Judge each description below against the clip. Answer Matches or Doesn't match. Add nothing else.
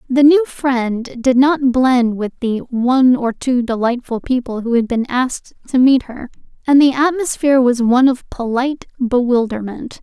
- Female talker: Matches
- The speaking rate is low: Doesn't match